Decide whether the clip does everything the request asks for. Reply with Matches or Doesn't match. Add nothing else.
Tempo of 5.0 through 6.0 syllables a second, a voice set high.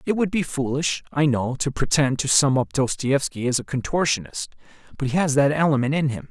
Doesn't match